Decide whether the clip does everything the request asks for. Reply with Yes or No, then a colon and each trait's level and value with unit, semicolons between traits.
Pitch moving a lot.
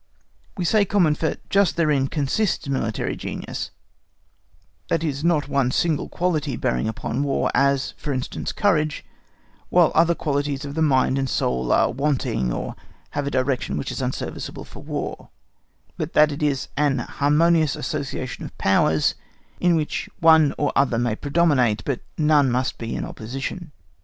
No: average, 3.4 semitones